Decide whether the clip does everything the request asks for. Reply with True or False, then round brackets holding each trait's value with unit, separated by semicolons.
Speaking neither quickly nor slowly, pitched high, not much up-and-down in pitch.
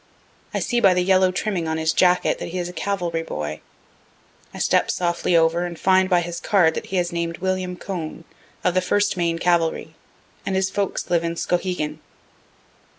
False (190 wpm; 175 Hz; 2.0 semitones)